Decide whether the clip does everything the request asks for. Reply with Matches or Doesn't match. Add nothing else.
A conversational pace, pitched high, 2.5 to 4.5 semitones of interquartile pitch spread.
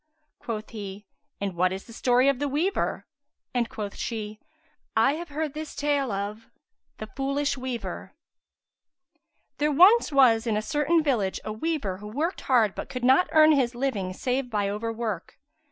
Doesn't match